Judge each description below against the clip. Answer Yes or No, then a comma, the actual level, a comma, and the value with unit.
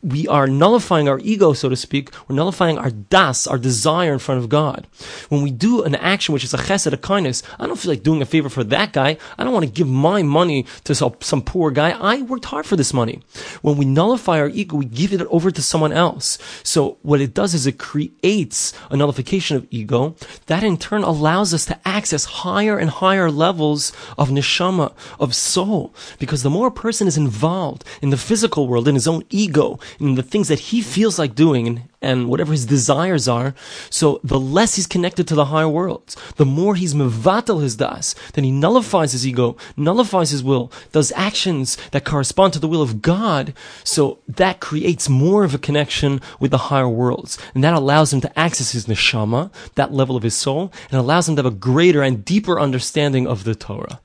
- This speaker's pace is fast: Yes, fast, 210 wpm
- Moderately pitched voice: Yes, medium, 150 Hz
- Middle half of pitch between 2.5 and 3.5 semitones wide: No, average, 4.7 semitones